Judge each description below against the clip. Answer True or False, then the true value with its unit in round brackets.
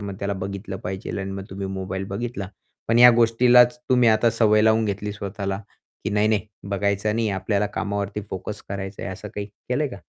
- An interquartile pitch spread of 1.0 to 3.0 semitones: True (2.4 semitones)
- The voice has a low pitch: True (100 Hz)